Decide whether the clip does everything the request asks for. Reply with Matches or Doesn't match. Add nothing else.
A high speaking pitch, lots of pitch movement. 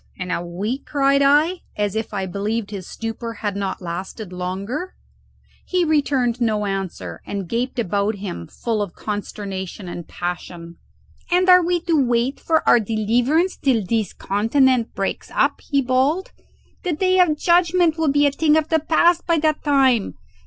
Matches